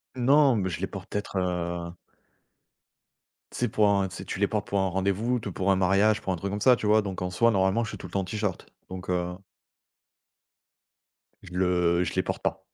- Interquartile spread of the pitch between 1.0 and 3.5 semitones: Yes, narrow, 2.5 semitones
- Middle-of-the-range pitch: No, very low, 95 Hz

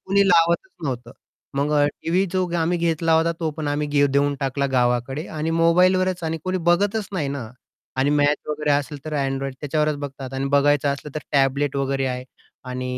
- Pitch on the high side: No, medium, 145 Hz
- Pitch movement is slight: No, average, 3.3 semitones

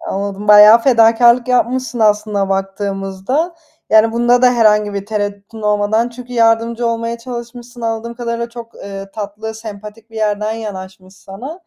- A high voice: Yes, high, 220 Hz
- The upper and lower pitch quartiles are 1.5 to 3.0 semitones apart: Yes, narrow, 2.5 semitones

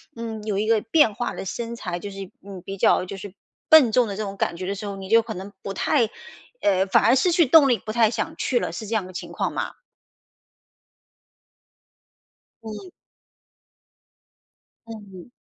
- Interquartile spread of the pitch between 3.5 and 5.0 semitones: No, average, 3.1 semitones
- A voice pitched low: No, high, 215 Hz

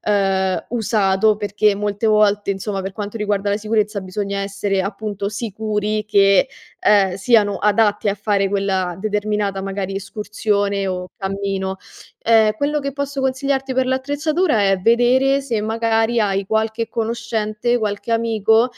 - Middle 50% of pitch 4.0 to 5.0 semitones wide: No, narrow, 2.4 semitones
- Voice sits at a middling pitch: No, high, 210 Hz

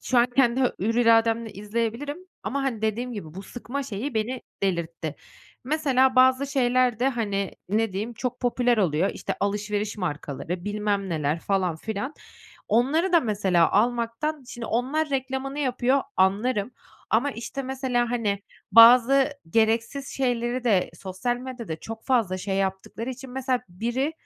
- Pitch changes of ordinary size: Yes, average, 4.2 semitones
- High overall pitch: Yes, high, 235 Hz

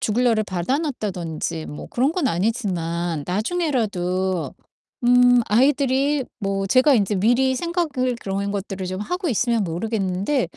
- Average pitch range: No, wide, 5.8 semitones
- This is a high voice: Yes, high, 215 Hz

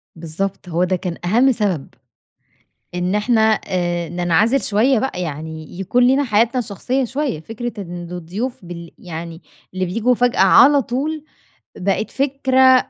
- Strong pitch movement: Yes, wide, 6.2 semitones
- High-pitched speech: Yes, high, 200 Hz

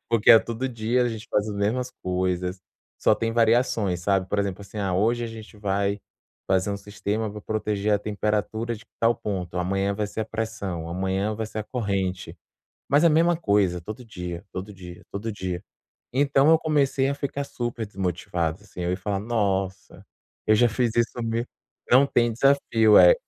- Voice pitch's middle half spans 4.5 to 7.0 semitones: No, average, 3.3 semitones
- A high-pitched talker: No, low, 105 Hz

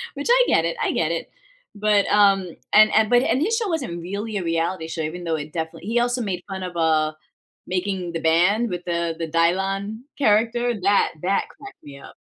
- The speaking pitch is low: No, high, 190 Hz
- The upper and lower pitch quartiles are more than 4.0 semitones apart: Yes, average, 4.6 semitones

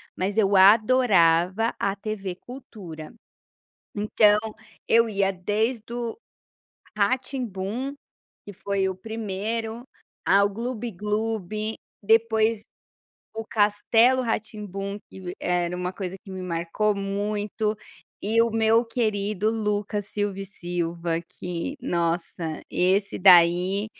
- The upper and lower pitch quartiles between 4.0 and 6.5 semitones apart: No, average, 3.0 semitones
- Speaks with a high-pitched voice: Yes, high, 205 Hz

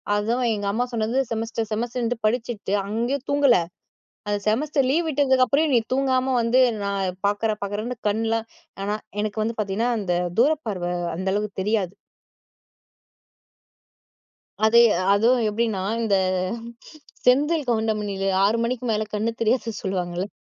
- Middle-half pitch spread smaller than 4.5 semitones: Yes, average, 3.2 semitones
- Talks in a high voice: Yes, high, 225 Hz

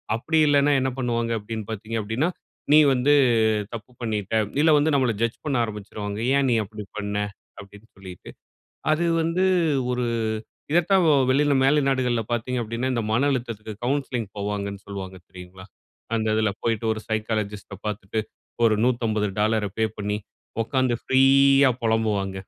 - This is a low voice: Yes, low, 115 Hz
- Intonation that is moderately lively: Yes, average, 3.9 semitones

